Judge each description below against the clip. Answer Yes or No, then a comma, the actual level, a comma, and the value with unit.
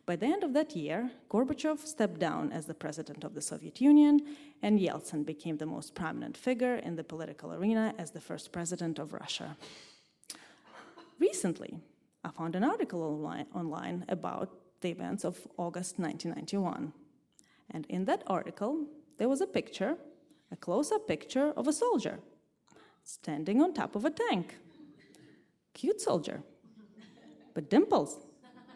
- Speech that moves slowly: No, average, 145 wpm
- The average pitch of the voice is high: Yes, high, 210 Hz